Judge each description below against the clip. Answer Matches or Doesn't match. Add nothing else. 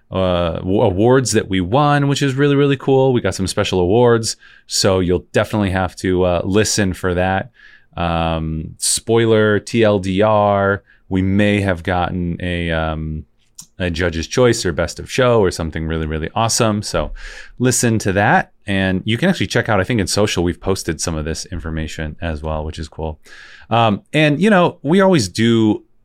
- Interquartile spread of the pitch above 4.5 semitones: Matches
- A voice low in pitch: Matches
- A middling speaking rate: Matches